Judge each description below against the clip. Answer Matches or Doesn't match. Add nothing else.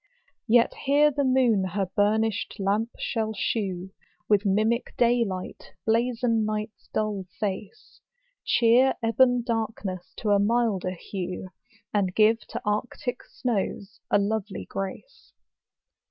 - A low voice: Doesn't match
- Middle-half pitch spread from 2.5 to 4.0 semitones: Matches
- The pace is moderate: Doesn't match